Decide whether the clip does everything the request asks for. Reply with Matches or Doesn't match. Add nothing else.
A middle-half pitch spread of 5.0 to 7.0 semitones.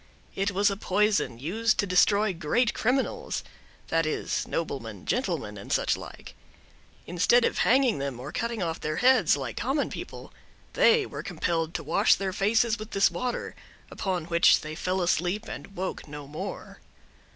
Matches